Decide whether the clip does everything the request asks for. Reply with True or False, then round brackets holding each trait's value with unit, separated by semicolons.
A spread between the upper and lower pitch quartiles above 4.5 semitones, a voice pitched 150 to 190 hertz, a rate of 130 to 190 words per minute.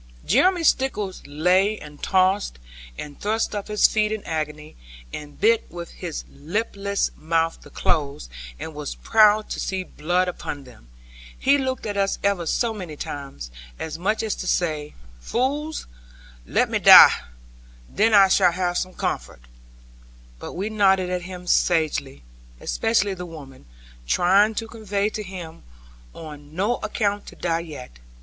True (5.1 semitones; 185 Hz; 150 wpm)